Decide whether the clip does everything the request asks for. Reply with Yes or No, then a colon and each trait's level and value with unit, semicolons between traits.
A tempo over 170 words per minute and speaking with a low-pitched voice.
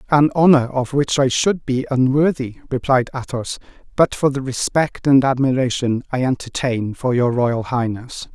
No: average, 160 wpm; low, 130 Hz